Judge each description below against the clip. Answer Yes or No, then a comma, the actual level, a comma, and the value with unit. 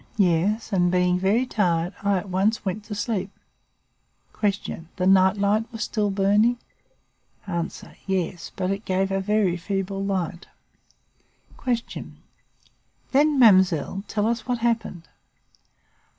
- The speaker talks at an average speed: No, slow, 125 wpm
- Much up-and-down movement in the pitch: No, average, 2.7 semitones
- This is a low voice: No, high, 195 Hz